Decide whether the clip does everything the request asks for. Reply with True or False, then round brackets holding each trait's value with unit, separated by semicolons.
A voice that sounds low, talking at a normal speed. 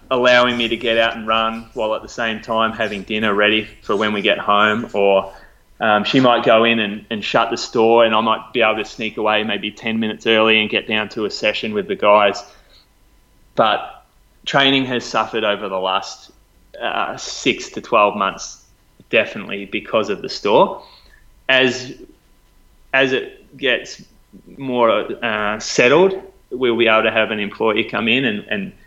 True (110 Hz; 180 wpm)